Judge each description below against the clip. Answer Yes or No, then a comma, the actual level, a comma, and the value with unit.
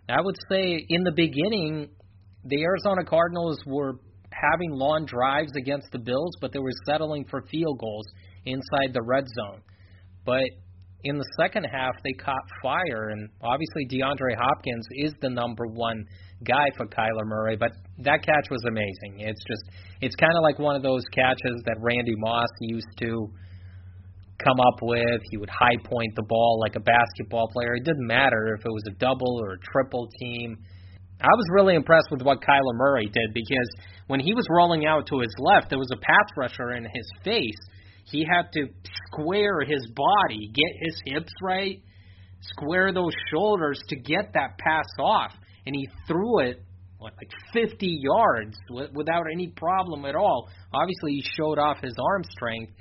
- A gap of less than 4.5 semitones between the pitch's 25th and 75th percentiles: No, wide, 5.5 semitones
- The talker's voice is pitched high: No, low, 125 Hz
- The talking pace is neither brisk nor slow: Yes, average, 175 wpm